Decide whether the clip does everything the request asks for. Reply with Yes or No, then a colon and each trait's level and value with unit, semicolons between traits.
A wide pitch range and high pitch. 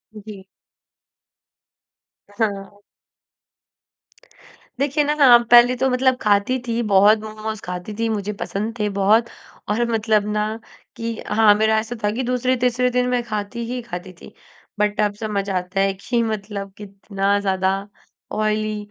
No: average, 2.9 semitones; high, 215 Hz